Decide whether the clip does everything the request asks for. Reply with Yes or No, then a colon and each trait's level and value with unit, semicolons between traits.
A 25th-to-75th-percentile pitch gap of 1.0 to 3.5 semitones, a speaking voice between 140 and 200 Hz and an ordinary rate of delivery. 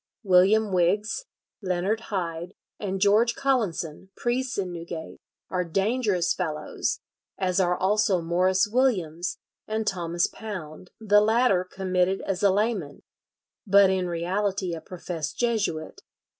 No: average, 3.1 semitones; high, 190 Hz; slow, 120 wpm